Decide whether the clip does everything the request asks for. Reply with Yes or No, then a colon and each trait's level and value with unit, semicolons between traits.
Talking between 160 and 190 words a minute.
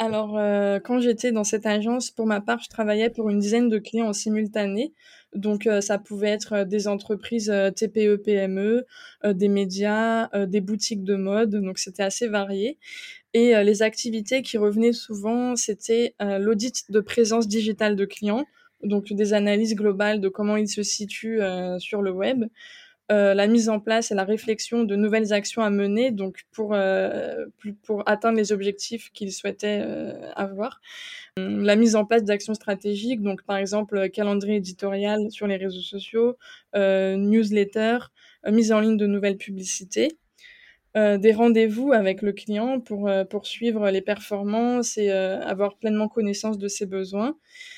Yes: average, 170 wpm